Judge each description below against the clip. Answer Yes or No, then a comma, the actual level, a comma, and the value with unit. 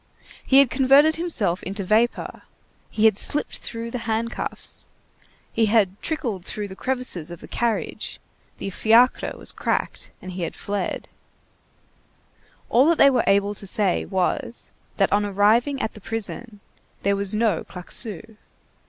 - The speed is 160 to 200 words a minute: No, average, 150 wpm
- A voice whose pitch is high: Yes, high, 220 Hz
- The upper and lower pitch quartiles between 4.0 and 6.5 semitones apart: No, average, 3.4 semitones